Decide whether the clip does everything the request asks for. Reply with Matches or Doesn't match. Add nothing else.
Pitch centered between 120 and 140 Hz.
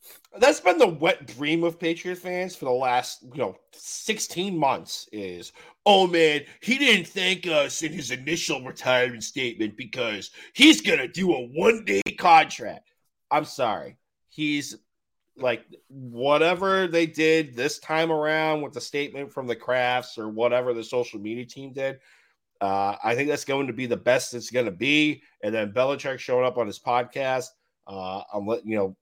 Matches